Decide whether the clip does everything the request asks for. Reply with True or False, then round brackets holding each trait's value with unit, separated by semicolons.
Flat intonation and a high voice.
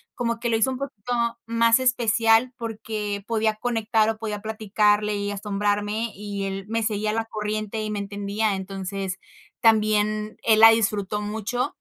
True (1.5 semitones; 215 Hz)